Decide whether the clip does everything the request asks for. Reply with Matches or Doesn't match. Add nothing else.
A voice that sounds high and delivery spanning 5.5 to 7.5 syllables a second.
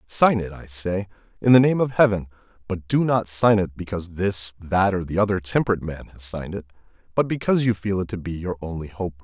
Doesn't match